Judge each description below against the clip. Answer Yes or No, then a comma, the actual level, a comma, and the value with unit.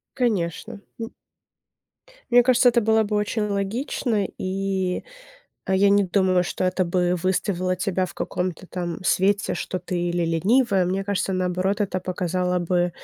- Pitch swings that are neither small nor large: No, narrow, 2.2 semitones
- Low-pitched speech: No, high, 190 Hz